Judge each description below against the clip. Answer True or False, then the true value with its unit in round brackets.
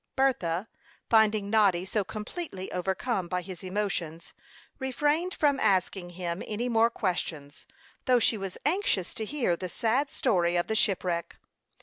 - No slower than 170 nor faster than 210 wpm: False (140 wpm)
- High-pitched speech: True (200 Hz)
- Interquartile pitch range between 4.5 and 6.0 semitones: True (4.8 semitones)